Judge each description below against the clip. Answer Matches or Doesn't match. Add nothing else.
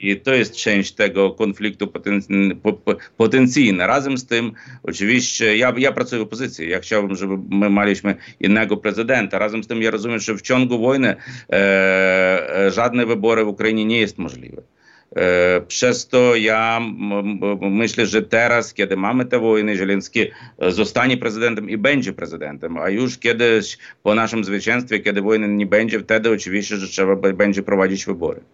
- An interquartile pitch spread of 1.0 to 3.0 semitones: Matches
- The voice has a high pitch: Doesn't match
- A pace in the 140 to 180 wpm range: Matches